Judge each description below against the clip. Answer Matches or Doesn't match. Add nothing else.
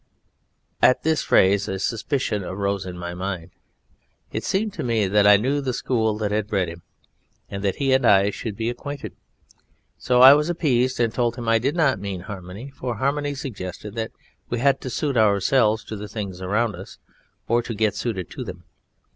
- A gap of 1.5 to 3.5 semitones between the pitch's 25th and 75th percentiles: Doesn't match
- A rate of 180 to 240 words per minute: Matches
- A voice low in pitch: Matches